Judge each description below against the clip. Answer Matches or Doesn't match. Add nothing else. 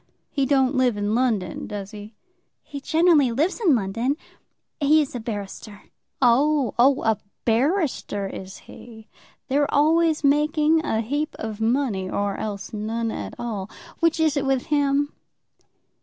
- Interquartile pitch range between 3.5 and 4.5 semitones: Doesn't match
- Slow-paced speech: Doesn't match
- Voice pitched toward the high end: Matches